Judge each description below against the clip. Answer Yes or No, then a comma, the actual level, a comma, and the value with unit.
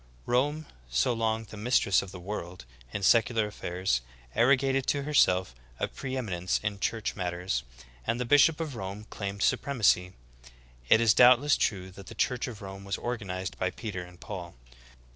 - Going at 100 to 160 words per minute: No, average, 170 wpm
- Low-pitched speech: Yes, low, 105 Hz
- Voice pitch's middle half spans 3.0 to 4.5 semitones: No, average, 5.0 semitones